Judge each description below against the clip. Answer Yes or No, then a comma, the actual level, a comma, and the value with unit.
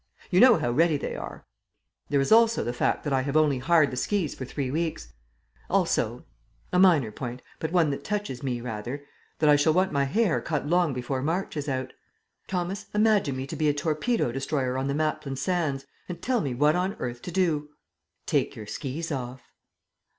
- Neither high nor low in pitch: Yes, medium, 150 Hz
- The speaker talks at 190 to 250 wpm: Yes, average, 200 wpm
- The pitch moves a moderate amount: Yes, average, 4.9 semitones